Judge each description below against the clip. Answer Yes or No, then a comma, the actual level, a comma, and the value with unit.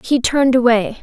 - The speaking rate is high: No, average, 175 wpm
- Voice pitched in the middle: No, high, 245 Hz